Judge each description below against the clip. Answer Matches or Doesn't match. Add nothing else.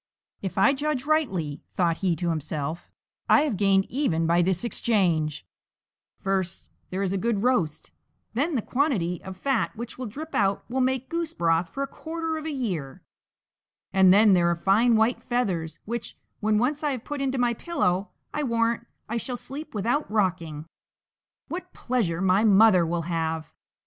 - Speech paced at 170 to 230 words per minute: Matches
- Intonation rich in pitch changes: Matches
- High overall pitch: Matches